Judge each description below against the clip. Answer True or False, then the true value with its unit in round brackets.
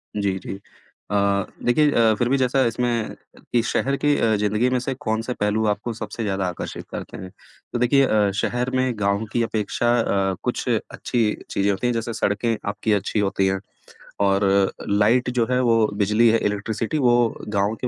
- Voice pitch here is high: False (115 Hz)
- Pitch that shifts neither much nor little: True (3.0 semitones)